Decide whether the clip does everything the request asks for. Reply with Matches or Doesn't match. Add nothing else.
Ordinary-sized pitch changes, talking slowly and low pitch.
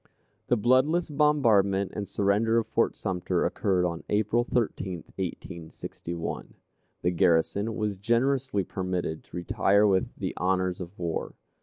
Matches